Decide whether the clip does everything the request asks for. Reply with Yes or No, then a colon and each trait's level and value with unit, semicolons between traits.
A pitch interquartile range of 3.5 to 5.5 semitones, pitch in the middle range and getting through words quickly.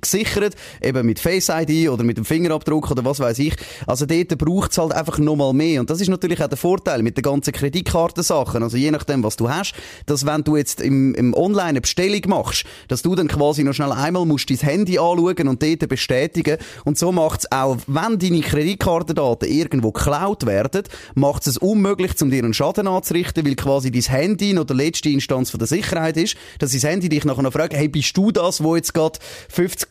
Yes: average, 4.1 semitones; medium, 150 Hz; fast, 215 wpm